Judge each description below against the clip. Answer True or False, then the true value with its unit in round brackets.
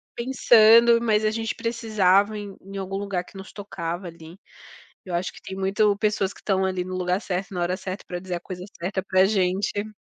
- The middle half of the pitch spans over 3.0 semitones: False (2.5 semitones)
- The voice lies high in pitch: True (195 Hz)